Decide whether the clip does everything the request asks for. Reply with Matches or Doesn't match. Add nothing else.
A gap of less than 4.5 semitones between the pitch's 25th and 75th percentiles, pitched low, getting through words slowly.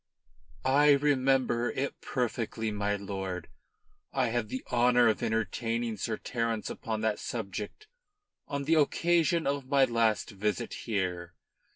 Matches